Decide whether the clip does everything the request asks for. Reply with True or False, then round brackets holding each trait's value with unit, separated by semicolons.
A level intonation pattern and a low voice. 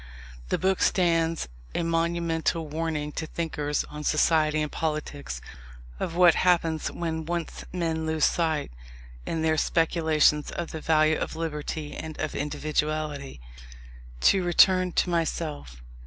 False (1.6 semitones; 160 Hz)